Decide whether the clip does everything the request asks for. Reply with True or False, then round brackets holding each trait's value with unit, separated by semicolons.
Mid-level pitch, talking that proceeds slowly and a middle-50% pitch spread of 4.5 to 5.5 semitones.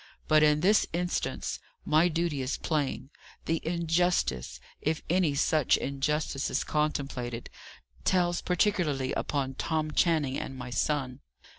False (150 Hz; 125 wpm; 3.8 semitones)